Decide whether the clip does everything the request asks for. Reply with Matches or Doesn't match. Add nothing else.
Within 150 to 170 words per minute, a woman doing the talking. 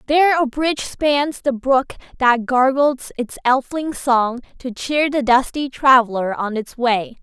Matches